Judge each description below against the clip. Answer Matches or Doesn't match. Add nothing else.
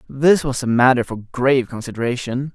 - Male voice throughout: Matches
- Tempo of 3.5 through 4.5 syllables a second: Doesn't match